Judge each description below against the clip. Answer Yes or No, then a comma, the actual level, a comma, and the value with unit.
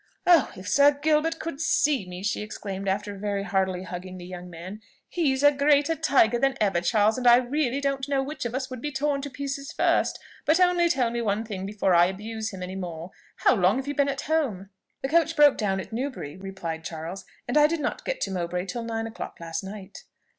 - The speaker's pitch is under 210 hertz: No, high, 230 Hz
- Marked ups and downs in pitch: Yes, wide, 6.8 semitones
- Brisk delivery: Yes, fast, 225 wpm